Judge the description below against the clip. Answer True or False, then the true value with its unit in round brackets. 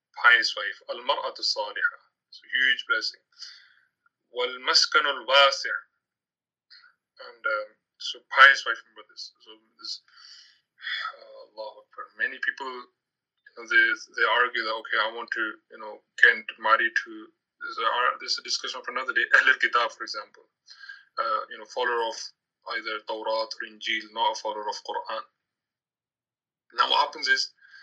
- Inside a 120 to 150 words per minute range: True (145 wpm)